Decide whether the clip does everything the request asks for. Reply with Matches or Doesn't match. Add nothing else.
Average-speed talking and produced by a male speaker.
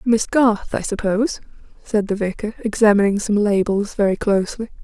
Doesn't match